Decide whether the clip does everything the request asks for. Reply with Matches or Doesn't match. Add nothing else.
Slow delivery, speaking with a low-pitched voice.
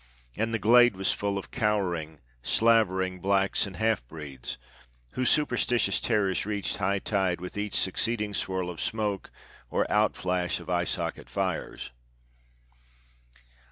Matches